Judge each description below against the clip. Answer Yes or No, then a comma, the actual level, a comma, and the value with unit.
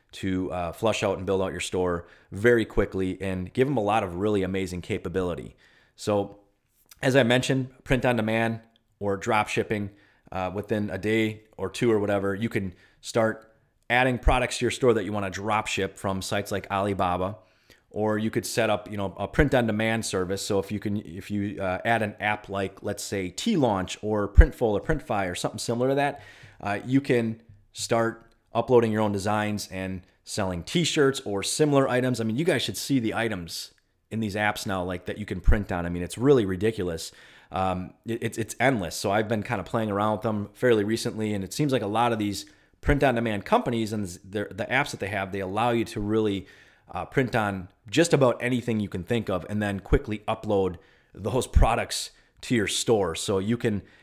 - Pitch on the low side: Yes, low, 105 Hz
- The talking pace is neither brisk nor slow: No, fast, 210 wpm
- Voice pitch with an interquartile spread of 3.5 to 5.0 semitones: No, average, 3.1 semitones